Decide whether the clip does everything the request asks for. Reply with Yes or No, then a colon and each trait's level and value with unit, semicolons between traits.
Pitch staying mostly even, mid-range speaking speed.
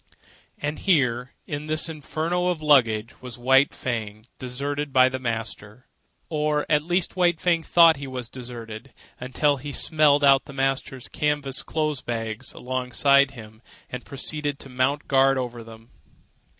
No: average, 3.3 semitones; average, 150 wpm